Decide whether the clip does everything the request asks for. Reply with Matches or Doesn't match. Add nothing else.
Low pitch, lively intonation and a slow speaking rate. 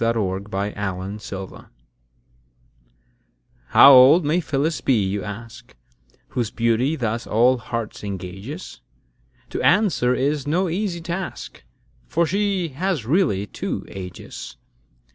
Matches